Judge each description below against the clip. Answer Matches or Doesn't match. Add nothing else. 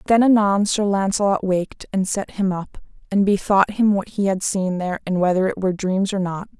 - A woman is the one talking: Matches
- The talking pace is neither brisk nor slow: Doesn't match